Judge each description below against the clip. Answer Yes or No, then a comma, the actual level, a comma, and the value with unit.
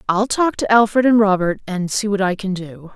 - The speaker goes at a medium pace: No, fast, 245 wpm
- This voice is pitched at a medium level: No, high, 205 Hz